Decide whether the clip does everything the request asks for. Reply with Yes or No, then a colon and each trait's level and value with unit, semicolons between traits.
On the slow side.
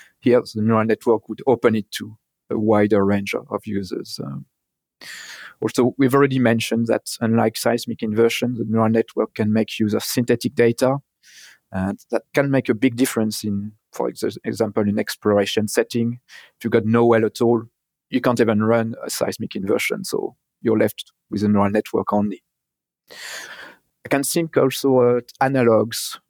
No: average, 170 wpm